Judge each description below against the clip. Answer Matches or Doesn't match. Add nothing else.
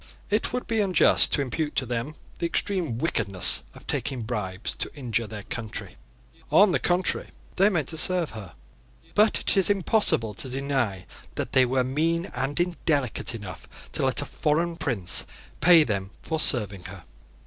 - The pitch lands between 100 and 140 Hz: Matches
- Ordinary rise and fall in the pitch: Doesn't match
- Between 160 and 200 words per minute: Matches